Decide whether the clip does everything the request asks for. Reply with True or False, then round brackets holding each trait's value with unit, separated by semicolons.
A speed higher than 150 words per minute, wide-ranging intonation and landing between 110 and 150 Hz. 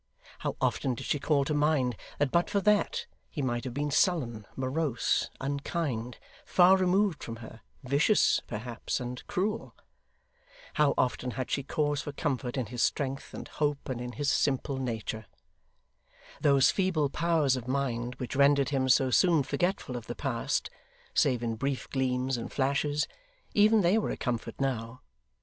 False (165 wpm; 3.3 semitones; 135 Hz)